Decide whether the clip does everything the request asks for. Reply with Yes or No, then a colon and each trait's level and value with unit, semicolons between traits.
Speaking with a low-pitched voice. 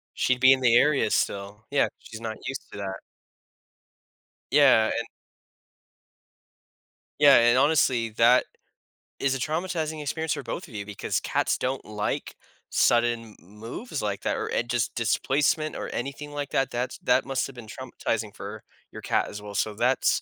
Yes: low, 125 Hz